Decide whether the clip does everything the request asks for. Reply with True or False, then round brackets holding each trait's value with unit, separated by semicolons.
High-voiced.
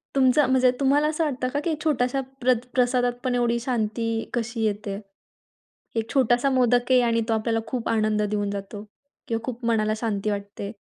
True (240 Hz)